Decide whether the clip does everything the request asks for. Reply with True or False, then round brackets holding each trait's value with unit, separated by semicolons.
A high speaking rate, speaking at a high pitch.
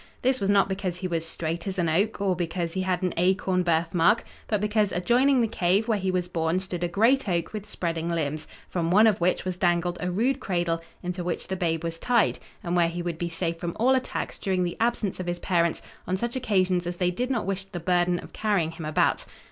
False (235 wpm; 180 Hz)